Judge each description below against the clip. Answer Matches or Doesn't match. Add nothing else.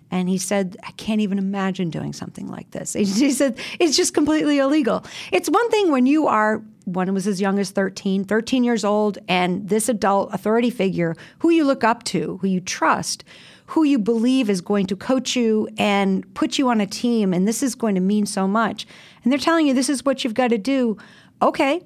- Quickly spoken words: Matches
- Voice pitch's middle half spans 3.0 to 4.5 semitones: Doesn't match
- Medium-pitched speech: Doesn't match